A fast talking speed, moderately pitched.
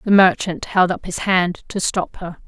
Yes: fast, 220 wpm; medium, 180 Hz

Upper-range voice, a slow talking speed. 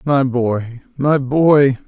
No: low, 135 Hz; slow, 130 wpm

